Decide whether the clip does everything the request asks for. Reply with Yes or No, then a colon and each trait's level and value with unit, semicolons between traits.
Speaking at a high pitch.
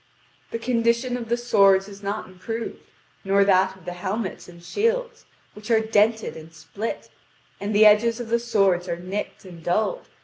Yes: high, 210 Hz